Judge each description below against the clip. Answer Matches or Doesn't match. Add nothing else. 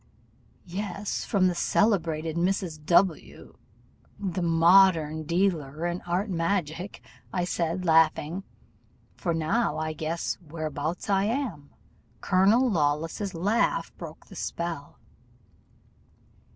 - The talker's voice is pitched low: Doesn't match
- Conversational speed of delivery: Doesn't match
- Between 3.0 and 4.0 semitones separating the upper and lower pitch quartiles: Matches